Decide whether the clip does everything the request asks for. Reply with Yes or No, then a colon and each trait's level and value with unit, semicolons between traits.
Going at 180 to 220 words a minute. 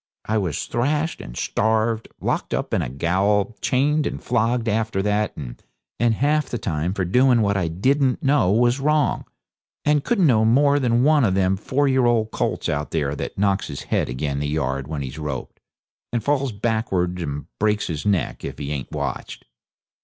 Yes: average, 185 wpm